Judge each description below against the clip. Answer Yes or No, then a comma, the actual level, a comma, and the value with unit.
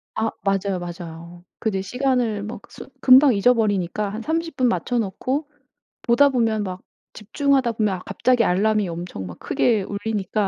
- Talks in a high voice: Yes, high, 215 Hz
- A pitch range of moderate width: Yes, average, 4.6 semitones